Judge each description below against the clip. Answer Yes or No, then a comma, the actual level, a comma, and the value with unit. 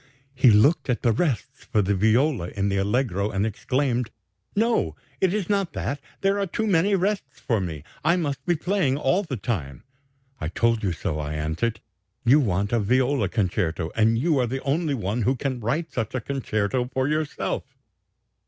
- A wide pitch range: Yes, wide, 6.5 semitones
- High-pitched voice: No, low, 125 Hz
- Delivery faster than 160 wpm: Yes, average, 185 wpm